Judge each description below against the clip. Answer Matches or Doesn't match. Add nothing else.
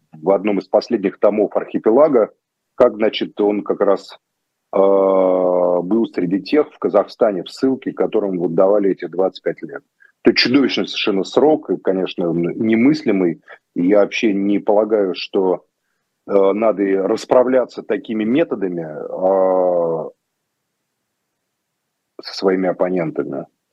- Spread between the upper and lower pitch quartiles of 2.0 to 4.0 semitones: Matches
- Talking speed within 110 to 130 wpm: Matches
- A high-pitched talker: Doesn't match